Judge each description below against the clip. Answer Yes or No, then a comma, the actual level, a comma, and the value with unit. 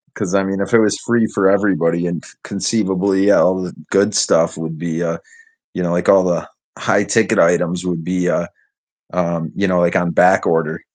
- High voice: No, very low, 90 Hz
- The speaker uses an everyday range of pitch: No, narrow, 2.3 semitones